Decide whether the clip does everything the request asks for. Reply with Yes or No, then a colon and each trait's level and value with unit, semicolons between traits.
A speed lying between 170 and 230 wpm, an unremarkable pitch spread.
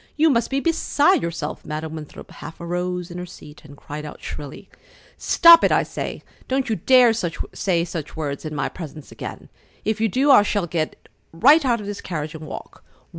No: average, 195 wpm; wide, 7.2 semitones